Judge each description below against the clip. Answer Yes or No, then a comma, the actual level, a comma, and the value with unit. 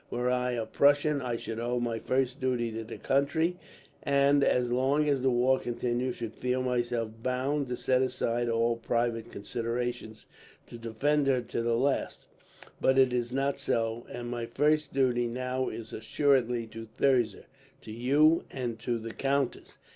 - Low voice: Yes, low, 125 Hz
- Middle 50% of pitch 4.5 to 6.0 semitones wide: No, narrow, 2.4 semitones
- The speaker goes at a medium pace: Yes, average, 170 wpm